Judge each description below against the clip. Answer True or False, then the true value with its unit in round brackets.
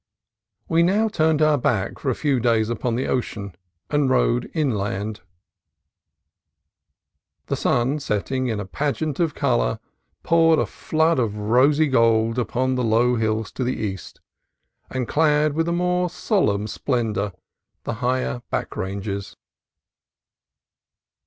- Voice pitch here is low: True (125 Hz)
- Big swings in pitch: True (5.7 semitones)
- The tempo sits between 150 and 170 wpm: False (135 wpm)